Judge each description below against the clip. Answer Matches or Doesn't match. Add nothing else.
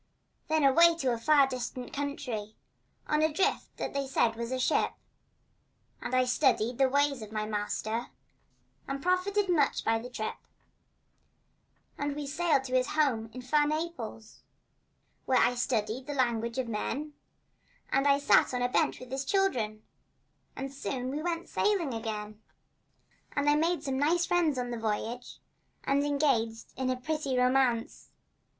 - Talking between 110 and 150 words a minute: Doesn't match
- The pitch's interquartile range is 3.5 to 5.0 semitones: Matches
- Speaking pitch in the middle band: Doesn't match